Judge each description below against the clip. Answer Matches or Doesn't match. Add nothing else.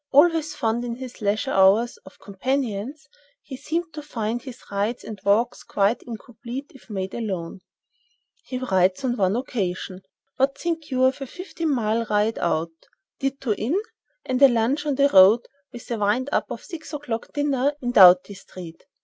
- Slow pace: Doesn't match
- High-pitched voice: Matches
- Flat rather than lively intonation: Doesn't match